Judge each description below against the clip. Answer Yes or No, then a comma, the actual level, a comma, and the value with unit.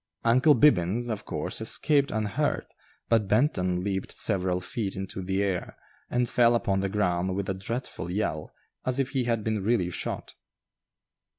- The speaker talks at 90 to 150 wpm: No, average, 160 wpm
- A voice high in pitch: No, low, 105 Hz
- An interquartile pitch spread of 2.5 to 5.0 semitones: Yes, average, 4.2 semitones